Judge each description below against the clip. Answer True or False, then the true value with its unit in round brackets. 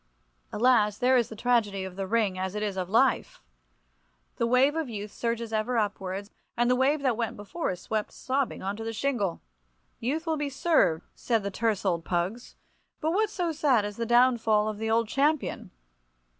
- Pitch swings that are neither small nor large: True (4.1 semitones)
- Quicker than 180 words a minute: True (195 wpm)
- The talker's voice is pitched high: True (230 Hz)